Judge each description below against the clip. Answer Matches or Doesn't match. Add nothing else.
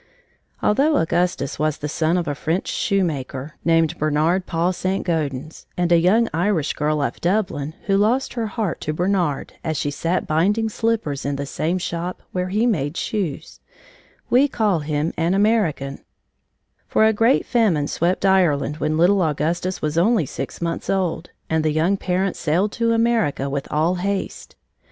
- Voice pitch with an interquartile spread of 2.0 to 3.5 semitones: Doesn't match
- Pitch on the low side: Doesn't match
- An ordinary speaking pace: Matches